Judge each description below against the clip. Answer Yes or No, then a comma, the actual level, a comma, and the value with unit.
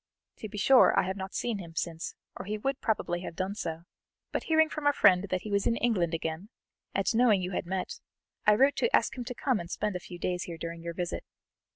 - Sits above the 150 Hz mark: Yes, high, 190 Hz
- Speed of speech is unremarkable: No, fast, 245 wpm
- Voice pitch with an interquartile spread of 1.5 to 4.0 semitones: No, average, 4.9 semitones